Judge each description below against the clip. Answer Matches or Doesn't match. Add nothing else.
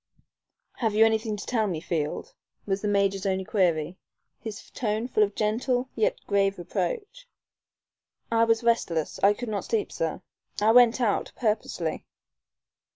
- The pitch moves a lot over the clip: Doesn't match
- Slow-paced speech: Doesn't match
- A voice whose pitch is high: Matches